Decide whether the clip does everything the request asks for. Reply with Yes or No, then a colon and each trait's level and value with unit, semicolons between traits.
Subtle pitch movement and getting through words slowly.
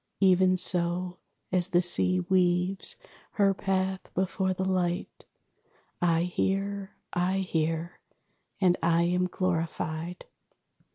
Yes: narrow, 1.4 semitones; slow, 105 wpm